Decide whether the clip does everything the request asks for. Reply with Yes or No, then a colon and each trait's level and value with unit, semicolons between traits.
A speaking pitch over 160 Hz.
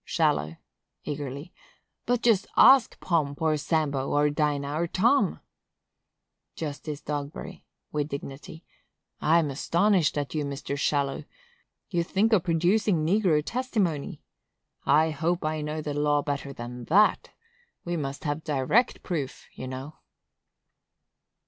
No: medium, 155 Hz